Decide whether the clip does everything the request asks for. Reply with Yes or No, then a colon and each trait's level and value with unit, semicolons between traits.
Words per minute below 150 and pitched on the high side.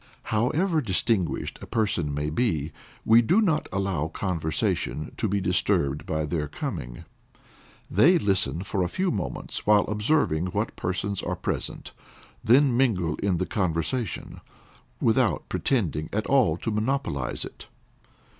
No: slow, 135 wpm; low, 100 Hz